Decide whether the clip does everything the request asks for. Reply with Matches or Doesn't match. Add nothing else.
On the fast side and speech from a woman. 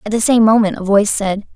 Matches